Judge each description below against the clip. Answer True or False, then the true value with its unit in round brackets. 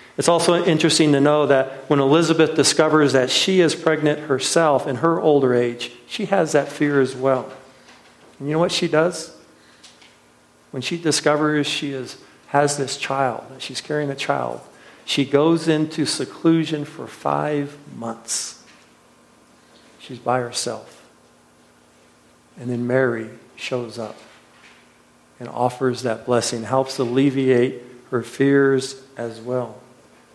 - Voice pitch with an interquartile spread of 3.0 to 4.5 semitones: True (3.5 semitones)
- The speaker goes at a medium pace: False (130 wpm)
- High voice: False (135 Hz)